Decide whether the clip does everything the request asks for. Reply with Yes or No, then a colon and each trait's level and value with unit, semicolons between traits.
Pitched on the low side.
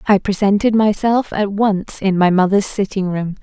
No: high, 200 Hz